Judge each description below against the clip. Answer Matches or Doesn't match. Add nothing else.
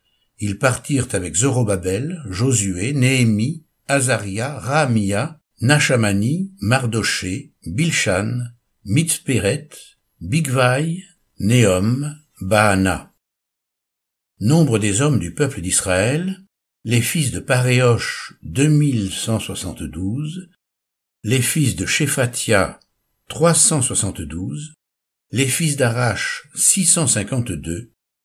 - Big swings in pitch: Matches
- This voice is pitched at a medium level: Doesn't match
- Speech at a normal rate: Doesn't match